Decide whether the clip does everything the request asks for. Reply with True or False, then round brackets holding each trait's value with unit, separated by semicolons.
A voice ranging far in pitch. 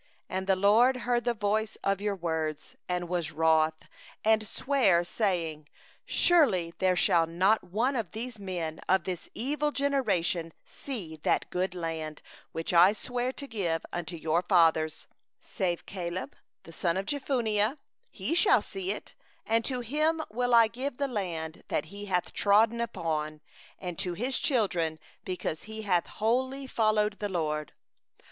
True (5.8 semitones)